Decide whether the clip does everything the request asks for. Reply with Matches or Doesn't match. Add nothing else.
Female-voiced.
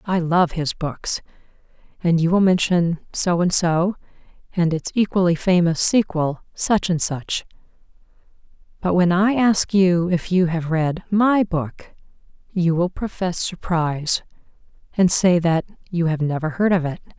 Matches